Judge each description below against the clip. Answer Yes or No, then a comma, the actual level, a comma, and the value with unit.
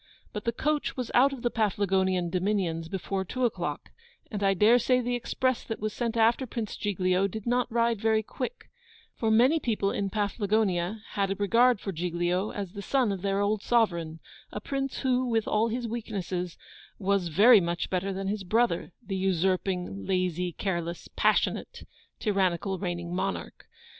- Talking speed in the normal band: Yes, average, 170 wpm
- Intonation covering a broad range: No, average, 4.0 semitones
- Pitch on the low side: No, high, 200 Hz